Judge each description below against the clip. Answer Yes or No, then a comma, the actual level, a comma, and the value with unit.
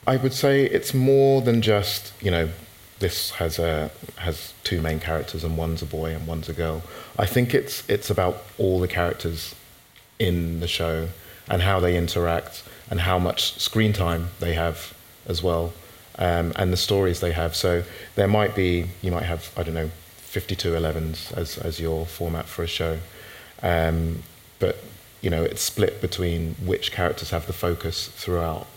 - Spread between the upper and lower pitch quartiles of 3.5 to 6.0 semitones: No, average, 2.8 semitones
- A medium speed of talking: Yes, average, 180 wpm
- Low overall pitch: Yes, very low, 85 Hz